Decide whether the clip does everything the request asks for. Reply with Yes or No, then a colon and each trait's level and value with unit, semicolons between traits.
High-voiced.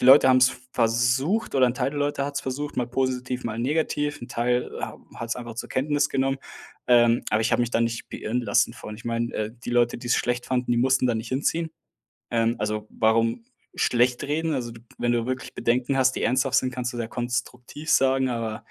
No: low, 125 Hz